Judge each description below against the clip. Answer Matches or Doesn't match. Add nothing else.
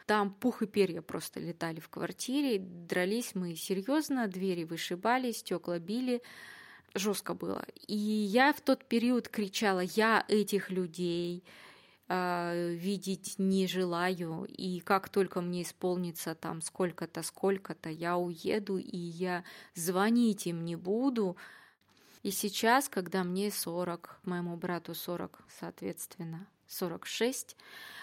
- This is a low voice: Doesn't match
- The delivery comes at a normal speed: Matches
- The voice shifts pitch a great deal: Doesn't match